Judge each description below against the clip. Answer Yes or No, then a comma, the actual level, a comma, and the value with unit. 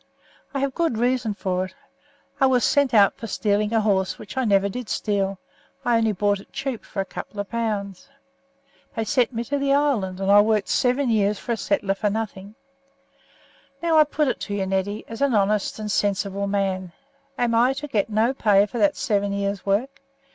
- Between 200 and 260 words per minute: Yes, fast, 205 wpm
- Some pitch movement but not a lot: Yes, average, 3.7 semitones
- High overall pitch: Yes, high, 210 Hz